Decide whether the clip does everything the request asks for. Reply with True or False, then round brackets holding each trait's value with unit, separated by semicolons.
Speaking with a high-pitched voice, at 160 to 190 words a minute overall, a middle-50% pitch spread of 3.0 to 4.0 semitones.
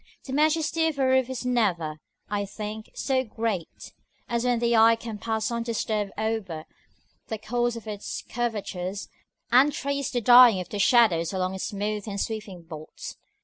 True (220 Hz; 170 wpm; 3.3 semitones)